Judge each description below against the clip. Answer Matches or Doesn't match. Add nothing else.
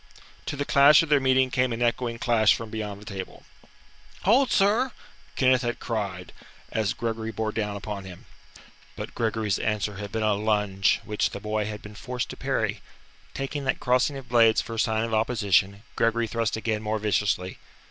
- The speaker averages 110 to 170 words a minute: Doesn't match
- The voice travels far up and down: Doesn't match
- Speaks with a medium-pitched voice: Doesn't match